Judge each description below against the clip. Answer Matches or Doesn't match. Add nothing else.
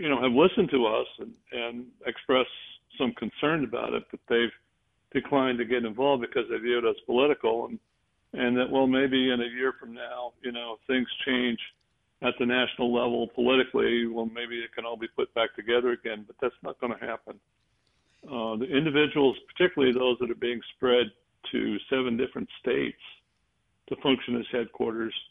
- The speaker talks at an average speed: Matches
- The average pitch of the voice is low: Matches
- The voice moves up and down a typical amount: Doesn't match